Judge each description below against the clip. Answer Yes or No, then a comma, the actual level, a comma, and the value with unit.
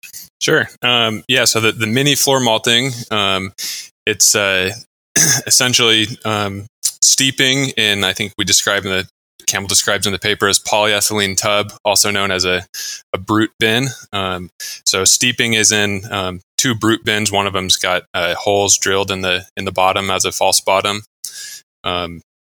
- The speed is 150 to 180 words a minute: Yes, average, 165 wpm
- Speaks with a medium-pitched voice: No, low, 105 Hz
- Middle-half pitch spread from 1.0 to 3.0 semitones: No, average, 3.5 semitones